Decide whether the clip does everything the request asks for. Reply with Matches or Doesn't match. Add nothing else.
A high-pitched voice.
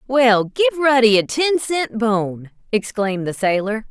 Matches